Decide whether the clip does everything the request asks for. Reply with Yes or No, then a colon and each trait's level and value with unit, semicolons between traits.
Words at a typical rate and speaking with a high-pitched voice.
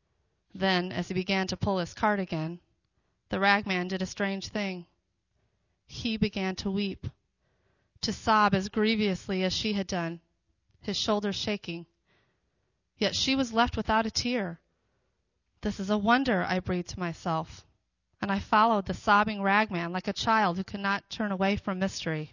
Yes: average, 165 wpm; high, 195 Hz